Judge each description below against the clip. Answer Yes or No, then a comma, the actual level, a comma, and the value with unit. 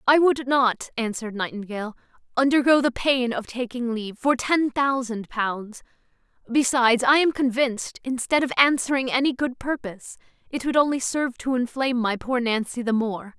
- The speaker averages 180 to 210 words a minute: No, average, 160 wpm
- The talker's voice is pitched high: Yes, very high, 250 Hz